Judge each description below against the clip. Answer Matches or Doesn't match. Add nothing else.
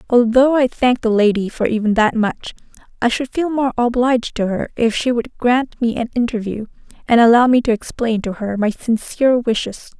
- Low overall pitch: Doesn't match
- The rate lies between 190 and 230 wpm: Matches